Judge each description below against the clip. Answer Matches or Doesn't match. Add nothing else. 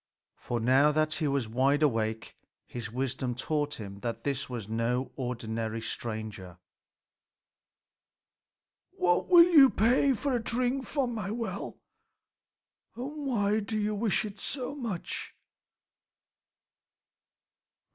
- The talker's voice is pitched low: Doesn't match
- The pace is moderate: Doesn't match